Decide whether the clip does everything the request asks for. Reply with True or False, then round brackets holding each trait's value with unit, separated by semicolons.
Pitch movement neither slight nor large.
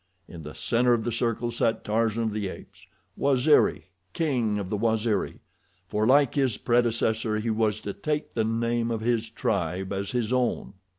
False (2.1 semitones)